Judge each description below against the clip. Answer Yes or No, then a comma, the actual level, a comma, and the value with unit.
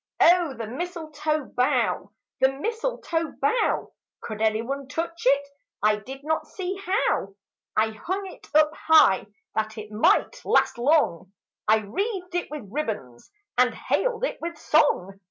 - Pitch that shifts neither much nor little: No, wide, 7.6 semitones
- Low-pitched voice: No, very high, 290 Hz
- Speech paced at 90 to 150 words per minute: Yes, average, 145 wpm